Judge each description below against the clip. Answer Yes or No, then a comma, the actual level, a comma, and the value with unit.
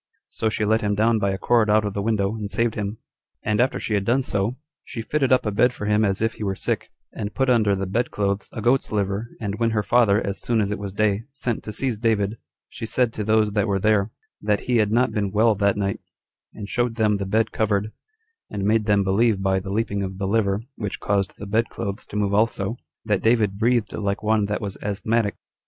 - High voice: No, low, 105 Hz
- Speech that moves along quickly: Yes, fast, 245 wpm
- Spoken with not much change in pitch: Yes, narrow, 2.2 semitones